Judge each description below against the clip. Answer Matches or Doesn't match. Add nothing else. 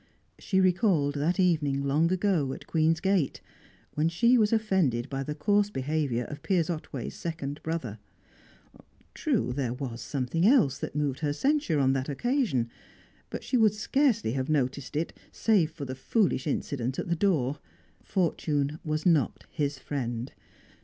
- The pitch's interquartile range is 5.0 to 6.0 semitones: Matches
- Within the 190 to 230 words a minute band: Doesn't match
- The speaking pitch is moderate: Matches